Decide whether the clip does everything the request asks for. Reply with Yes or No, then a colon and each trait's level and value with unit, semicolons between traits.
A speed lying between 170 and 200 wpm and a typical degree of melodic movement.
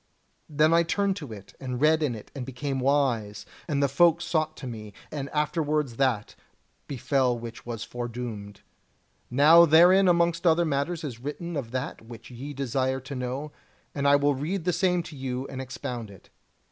Yes: average, 180 wpm; average, 4.2 semitones